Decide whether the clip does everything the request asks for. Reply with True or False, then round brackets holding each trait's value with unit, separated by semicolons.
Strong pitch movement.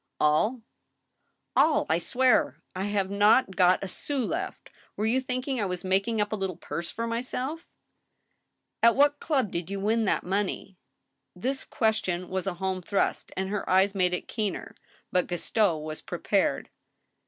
False (4.1 semitones)